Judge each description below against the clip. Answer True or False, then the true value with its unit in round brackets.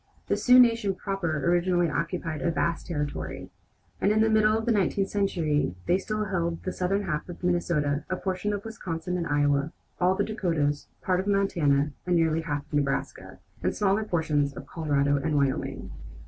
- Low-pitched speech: False (175 Hz)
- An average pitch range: True (4.7 semitones)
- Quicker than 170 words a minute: True (180 wpm)